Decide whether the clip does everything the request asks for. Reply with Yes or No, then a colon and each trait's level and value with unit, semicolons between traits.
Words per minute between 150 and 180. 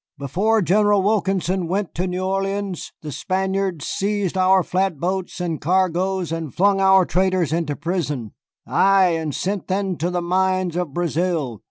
Yes: average, 155 wpm